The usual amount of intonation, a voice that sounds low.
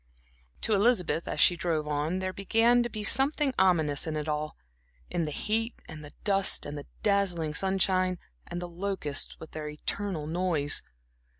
No: average, 4.6 semitones; medium, 180 Hz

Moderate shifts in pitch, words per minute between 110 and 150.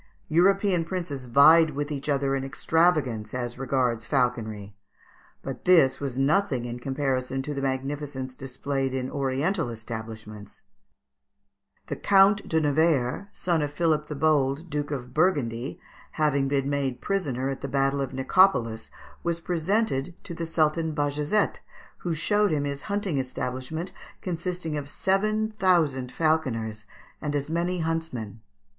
Yes: average, 4.2 semitones; average, 140 wpm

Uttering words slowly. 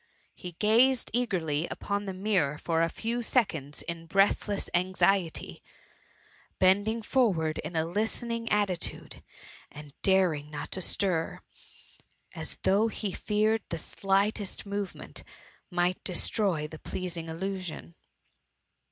Yes: slow, 115 wpm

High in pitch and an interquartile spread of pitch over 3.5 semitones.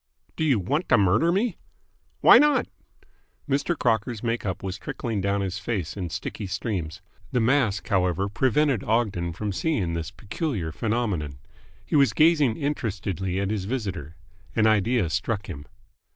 No: low, 105 Hz; average, 5.2 semitones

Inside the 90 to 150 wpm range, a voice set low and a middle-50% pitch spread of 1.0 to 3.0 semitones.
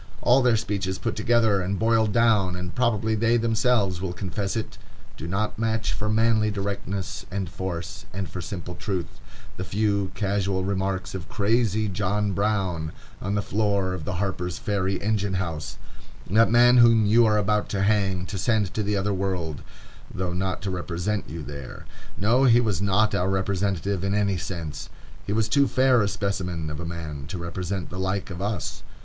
No: average, 175 wpm; low, 100 Hz; average, 2.7 semitones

